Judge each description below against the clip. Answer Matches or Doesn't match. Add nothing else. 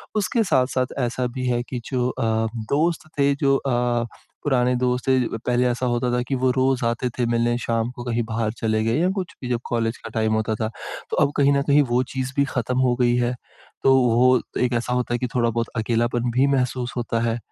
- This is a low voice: Matches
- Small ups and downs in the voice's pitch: Matches